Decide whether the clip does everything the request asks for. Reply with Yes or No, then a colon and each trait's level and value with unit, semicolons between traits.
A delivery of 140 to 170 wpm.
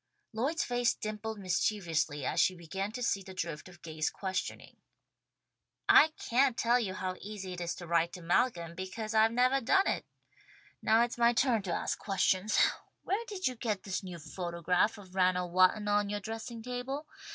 No: average, 180 wpm